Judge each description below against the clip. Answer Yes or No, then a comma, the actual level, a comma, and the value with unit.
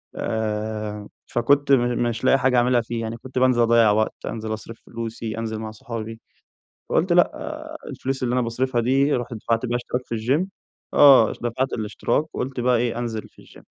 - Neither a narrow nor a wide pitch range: No, narrow, 2.3 semitones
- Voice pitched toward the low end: Yes, low, 120 Hz